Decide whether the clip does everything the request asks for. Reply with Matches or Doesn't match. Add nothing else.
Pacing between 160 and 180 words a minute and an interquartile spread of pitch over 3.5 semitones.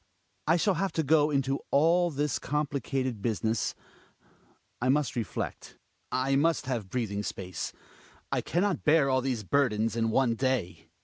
Matches